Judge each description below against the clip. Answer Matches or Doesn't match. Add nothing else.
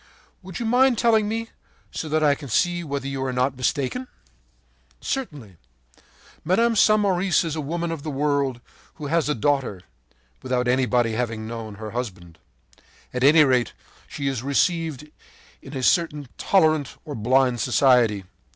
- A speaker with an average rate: Matches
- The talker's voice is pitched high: Doesn't match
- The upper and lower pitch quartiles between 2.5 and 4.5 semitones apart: Doesn't match